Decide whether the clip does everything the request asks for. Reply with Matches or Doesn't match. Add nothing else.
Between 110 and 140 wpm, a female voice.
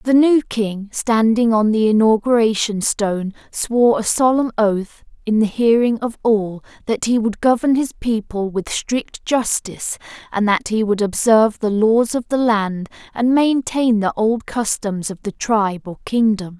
Doesn't match